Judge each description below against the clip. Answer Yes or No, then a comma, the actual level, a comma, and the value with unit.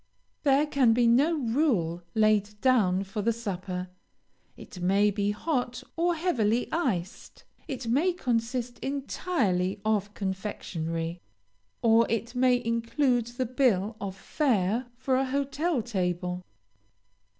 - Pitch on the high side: Yes, high, 230 Hz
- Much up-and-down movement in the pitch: No, average, 5.0 semitones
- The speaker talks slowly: Yes, slow, 120 wpm